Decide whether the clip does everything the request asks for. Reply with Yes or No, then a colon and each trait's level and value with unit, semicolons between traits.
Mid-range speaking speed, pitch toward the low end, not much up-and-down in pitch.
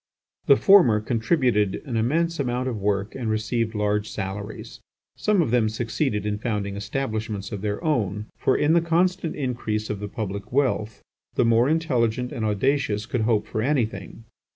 No: average, 165 wpm; low, 115 Hz; average, 4.2 semitones